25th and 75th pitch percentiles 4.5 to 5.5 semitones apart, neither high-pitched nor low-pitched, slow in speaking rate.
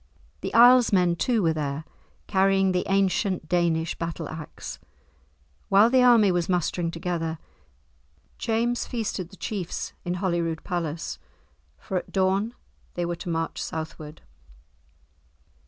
No: average, 3.2 semitones; medium, 180 Hz; slow, 125 wpm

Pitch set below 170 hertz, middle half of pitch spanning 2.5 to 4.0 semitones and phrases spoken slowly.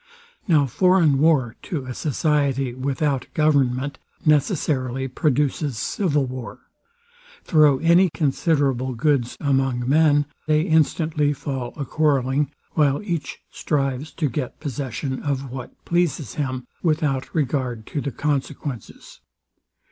Yes: medium, 140 Hz; average, 2.8 semitones; slow, 115 wpm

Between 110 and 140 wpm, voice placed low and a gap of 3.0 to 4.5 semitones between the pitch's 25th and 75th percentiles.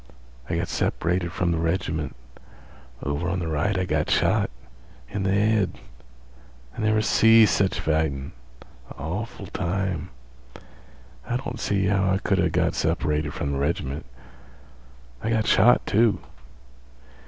Yes: slow, 135 wpm; very low, 95 Hz; average, 4.2 semitones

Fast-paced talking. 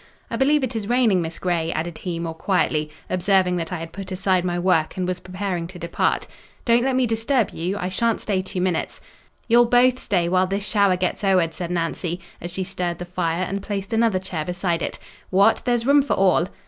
Yes: fast, 210 wpm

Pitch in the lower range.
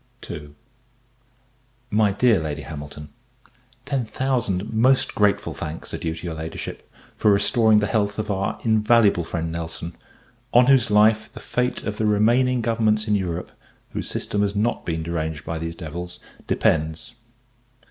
Yes: low, 105 Hz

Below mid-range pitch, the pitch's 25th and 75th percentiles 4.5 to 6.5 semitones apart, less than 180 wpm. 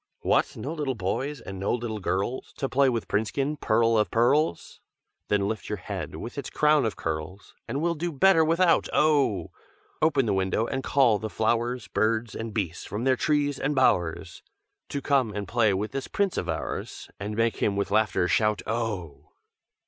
No: low, 115 Hz; average, 5.3 semitones; average, 185 wpm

